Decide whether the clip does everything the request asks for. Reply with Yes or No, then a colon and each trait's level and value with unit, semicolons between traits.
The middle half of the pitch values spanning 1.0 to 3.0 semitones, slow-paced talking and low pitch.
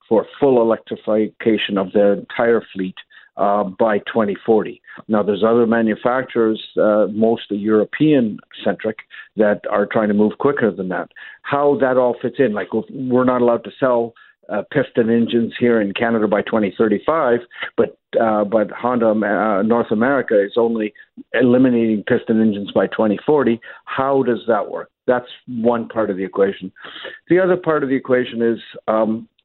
No: narrow, 2.6 semitones; average, 155 wpm; low, 115 Hz